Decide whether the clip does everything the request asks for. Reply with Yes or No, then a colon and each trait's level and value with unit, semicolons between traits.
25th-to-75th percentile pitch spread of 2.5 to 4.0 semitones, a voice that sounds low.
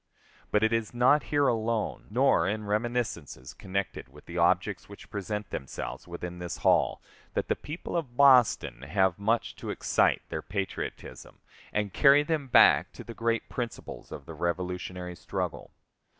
No: average, 5.0 semitones; low, 105 Hz